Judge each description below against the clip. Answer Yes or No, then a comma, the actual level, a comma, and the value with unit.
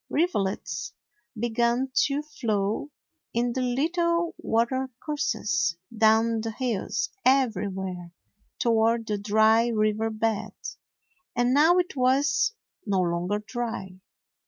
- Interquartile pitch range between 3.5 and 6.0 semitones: Yes, average, 3.8 semitones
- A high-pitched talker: Yes, high, 225 Hz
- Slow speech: Yes, slow, 100 wpm